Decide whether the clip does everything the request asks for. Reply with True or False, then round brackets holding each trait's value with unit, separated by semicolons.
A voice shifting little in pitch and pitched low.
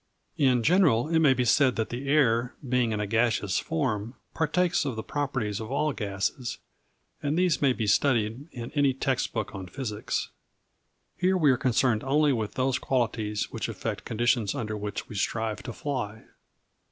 False (4.3 semitones; 125 Hz)